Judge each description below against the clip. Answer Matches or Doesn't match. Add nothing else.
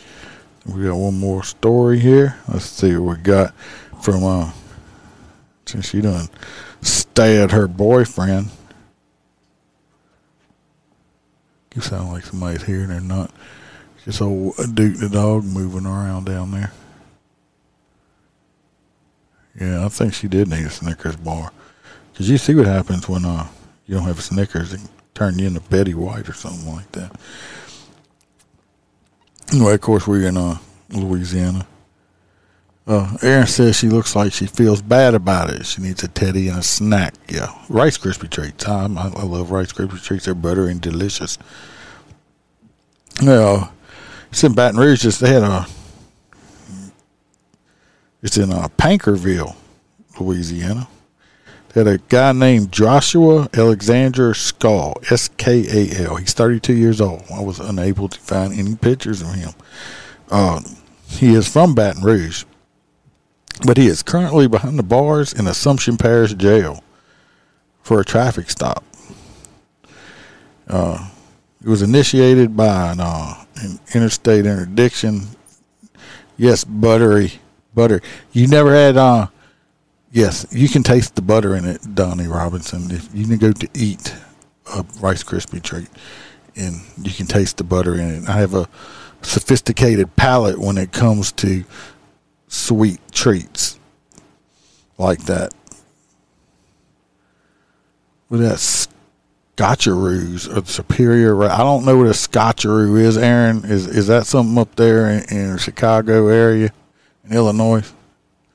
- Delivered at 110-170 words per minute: Matches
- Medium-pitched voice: Doesn't match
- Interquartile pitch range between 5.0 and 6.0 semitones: Doesn't match